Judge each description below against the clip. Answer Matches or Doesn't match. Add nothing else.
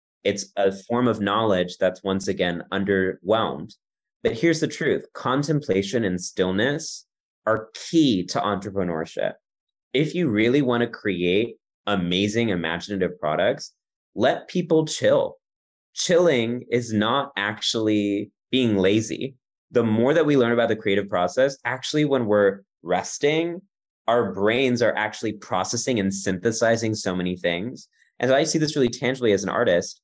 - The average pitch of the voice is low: Matches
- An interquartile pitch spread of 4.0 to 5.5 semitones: Matches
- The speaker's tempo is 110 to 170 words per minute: Matches